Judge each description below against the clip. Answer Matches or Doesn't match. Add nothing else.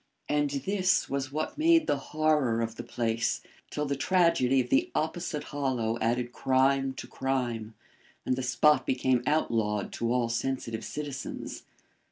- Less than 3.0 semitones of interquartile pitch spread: Doesn't match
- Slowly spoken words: Doesn't match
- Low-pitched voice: Matches